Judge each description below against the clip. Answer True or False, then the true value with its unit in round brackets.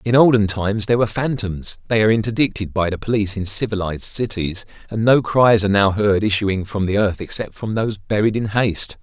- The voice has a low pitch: True (105 Hz)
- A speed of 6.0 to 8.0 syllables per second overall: True (6.1 syllables/s)